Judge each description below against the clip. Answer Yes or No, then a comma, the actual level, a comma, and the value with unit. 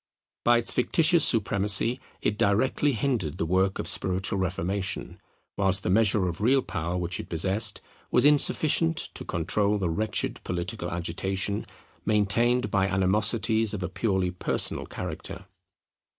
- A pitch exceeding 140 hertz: No, low, 100 Hz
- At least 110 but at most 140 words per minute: Yes, slow, 135 wpm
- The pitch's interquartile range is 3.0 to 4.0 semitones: Yes, average, 3.5 semitones